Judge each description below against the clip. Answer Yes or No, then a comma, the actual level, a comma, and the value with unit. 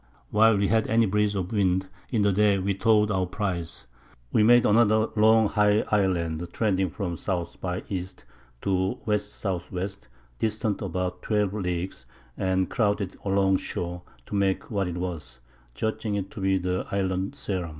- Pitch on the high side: No, low, 100 Hz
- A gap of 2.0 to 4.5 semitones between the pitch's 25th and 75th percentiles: Yes, narrow, 2.4 semitones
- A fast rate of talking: No, average, 160 wpm